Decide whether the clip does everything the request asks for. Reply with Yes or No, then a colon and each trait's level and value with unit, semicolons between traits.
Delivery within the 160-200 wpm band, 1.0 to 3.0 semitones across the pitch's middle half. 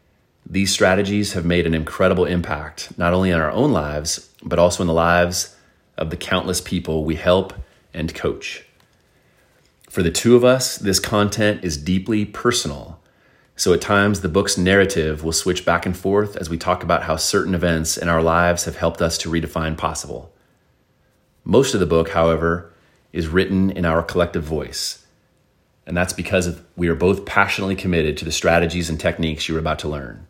Yes: average, 180 wpm; narrow, 2.6 semitones